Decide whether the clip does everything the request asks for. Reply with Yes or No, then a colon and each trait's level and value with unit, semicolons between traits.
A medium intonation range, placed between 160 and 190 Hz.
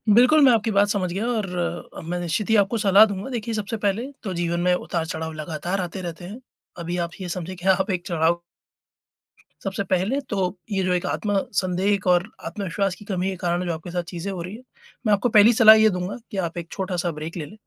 Yes: average, 3.0 semitones; medium, 185 Hz